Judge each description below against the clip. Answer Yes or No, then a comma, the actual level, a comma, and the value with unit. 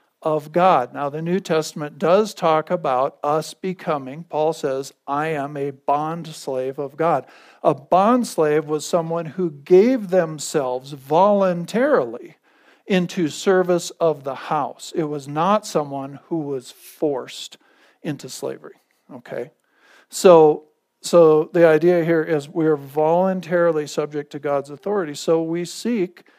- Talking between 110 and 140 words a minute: Yes, slow, 135 wpm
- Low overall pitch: No, medium, 160 Hz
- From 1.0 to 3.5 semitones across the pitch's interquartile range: Yes, average, 3.1 semitones